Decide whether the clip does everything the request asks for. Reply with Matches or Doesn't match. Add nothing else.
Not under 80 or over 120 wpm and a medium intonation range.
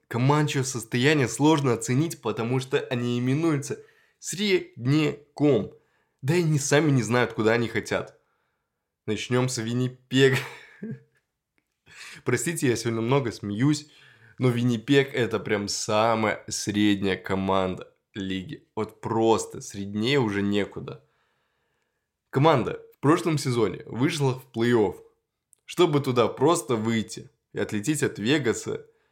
Matches